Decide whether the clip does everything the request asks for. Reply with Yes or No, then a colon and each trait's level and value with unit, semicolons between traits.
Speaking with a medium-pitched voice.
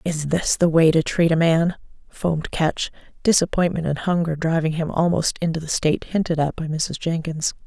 Yes: medium, 165 Hz